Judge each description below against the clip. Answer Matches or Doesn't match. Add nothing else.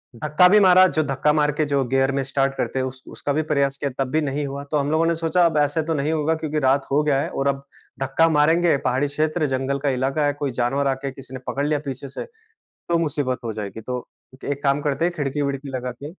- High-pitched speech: Doesn't match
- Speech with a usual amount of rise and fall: Doesn't match